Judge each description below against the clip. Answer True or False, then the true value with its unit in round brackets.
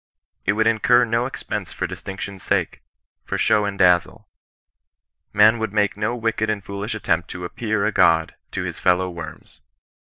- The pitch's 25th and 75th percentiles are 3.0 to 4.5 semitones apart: True (3.3 semitones)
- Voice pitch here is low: True (105 Hz)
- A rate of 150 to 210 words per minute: True (175 wpm)